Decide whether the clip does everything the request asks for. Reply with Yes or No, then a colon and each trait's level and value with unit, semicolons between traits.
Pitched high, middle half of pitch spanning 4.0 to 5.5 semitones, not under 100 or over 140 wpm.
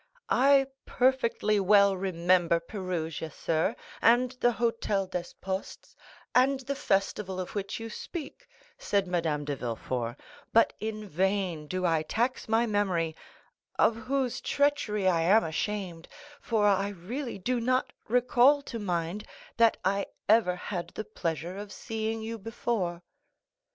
Yes: high, 205 Hz; average, 4.6 semitones; slow, 135 wpm